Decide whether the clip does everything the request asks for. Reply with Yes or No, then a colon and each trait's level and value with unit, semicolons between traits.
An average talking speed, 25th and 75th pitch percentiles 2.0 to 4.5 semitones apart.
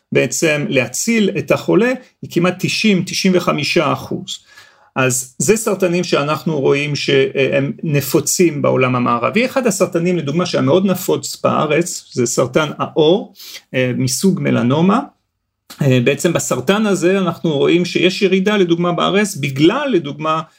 No: average, 115 wpm; average, 5.0 semitones